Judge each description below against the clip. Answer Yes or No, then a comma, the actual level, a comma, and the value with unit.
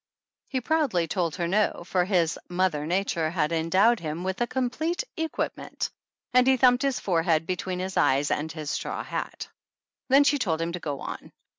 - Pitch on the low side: No, medium, 185 Hz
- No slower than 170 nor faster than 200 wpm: Yes, average, 185 wpm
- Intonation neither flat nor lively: No, wide, 7.1 semitones